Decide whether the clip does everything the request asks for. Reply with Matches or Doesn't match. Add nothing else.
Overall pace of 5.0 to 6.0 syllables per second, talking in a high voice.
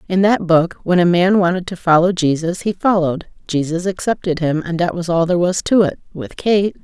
Doesn't match